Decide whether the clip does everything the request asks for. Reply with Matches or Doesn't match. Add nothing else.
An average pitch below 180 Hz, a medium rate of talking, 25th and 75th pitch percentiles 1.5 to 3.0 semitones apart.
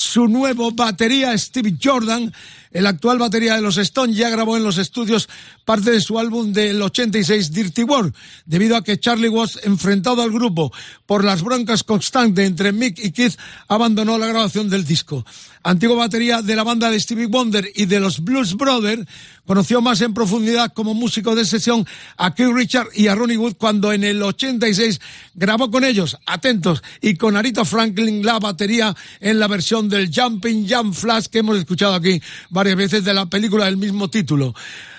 Doesn't match